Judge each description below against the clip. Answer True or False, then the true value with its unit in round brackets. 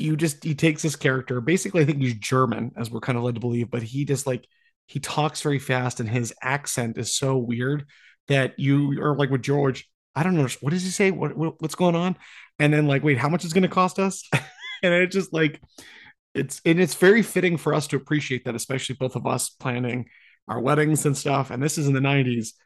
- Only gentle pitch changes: False (3.8 semitones)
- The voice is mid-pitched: True (145 Hz)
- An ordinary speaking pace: False (235 wpm)